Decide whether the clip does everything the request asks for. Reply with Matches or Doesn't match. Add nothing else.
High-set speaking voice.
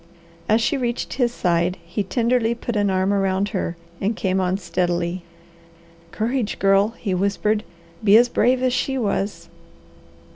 Matches